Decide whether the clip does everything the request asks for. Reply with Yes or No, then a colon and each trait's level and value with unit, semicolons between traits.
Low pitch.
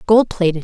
No: high, 190 Hz